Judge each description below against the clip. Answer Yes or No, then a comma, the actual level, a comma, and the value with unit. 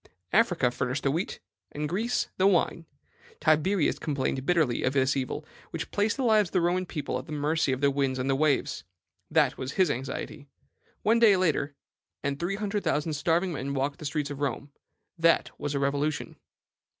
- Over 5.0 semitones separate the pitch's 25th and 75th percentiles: No, average, 4.4 semitones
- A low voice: No, medium, 150 Hz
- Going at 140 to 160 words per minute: No, average, 185 wpm